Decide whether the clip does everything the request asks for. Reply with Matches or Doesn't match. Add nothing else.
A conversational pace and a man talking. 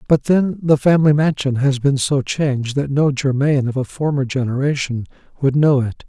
Matches